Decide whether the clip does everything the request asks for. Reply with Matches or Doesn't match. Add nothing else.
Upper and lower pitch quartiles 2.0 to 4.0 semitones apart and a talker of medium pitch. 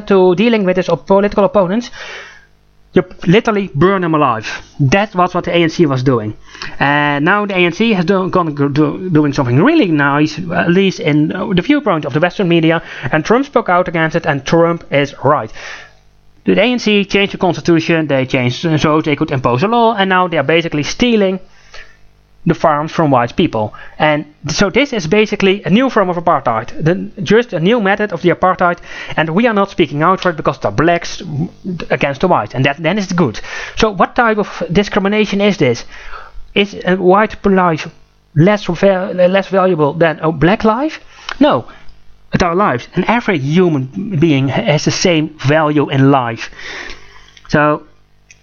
Doesn't match